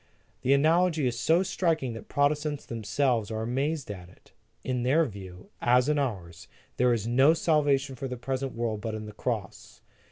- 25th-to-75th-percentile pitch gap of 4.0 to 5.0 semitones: Yes, average, 4.5 semitones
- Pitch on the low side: Yes, low, 125 Hz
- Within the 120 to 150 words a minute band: No, average, 180 wpm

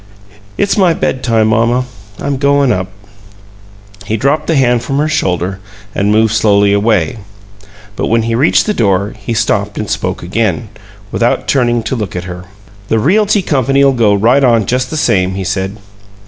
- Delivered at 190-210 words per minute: No, average, 170 wpm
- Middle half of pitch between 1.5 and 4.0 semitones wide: No, average, 5.0 semitones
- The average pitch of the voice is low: Yes, low, 115 Hz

